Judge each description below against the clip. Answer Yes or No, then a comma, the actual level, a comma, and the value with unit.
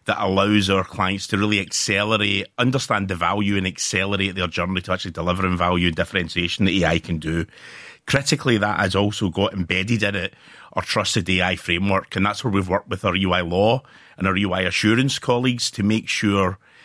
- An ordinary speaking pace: Yes, average, 190 wpm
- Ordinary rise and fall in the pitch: No, narrow, 2.3 semitones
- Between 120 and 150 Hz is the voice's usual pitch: No, very low, 95 Hz